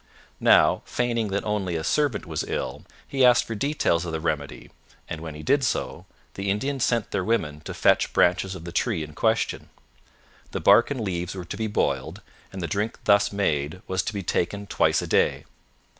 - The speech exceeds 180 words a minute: Yes, average, 200 wpm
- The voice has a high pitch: No, low, 100 Hz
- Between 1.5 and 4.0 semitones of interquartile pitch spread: No, wide, 5.4 semitones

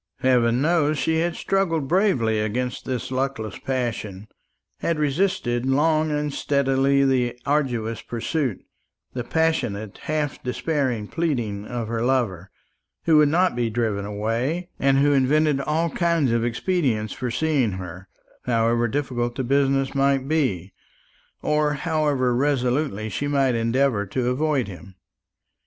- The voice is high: No, low, 130 Hz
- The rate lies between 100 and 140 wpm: Yes, slow, 135 wpm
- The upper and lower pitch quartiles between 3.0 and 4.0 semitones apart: No, average, 4.4 semitones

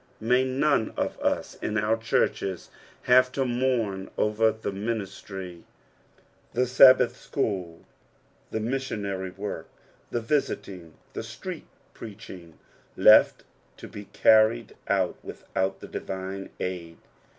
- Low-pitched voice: Yes, low, 105 Hz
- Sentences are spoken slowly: Yes, slow, 115 wpm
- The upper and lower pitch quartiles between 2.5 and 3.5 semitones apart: No, average, 4.2 semitones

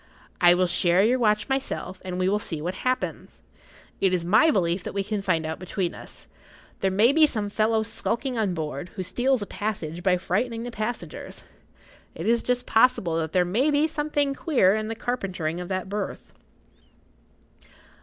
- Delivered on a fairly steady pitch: No, average, 5.0 semitones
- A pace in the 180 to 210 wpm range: Yes, average, 185 wpm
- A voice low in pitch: No, high, 205 Hz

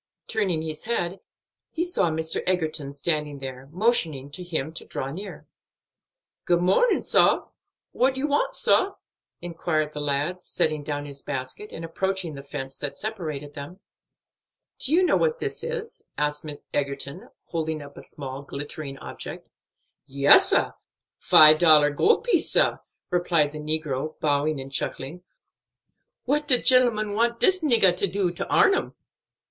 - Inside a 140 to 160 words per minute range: Yes, average, 150 wpm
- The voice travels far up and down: Yes, wide, 6.0 semitones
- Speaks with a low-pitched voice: No, medium, 160 Hz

